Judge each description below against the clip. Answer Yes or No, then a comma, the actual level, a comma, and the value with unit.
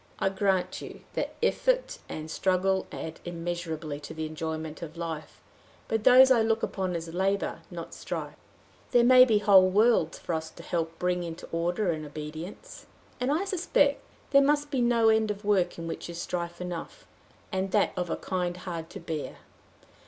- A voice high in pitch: No, medium, 180 Hz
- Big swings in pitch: No, average, 5.0 semitones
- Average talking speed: Yes, average, 180 wpm